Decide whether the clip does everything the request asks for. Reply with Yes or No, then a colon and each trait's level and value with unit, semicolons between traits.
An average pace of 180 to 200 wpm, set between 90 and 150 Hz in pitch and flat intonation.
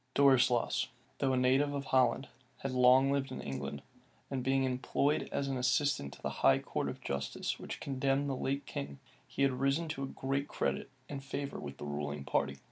Yes: average, 190 wpm; low, 135 Hz; narrow, 2.0 semitones